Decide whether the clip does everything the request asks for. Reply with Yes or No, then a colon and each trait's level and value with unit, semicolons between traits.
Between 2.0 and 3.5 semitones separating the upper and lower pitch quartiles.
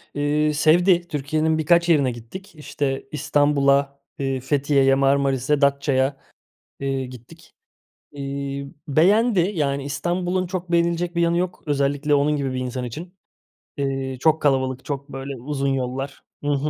Yes: average, 2.8 semitones